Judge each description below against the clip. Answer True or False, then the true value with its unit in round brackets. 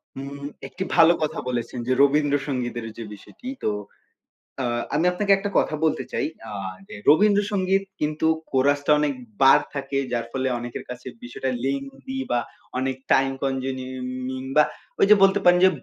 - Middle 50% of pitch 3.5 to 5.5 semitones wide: False (3.0 semitones)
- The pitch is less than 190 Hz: True (135 Hz)